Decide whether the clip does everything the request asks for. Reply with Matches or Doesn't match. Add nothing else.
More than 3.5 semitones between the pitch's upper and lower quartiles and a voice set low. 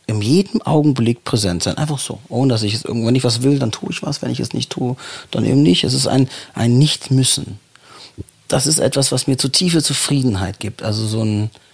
Matches